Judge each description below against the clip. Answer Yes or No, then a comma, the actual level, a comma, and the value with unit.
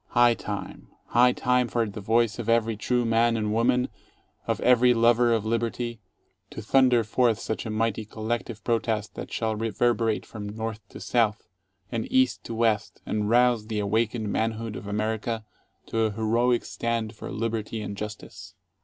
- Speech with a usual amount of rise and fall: No, narrow, 1.7 semitones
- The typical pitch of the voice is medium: No, low, 115 Hz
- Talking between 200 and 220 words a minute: No, average, 165 wpm